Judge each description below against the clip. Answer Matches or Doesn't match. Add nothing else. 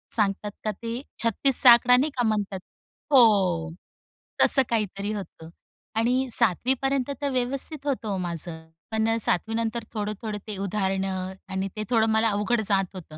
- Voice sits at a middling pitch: Doesn't match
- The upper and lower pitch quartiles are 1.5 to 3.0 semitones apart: Doesn't match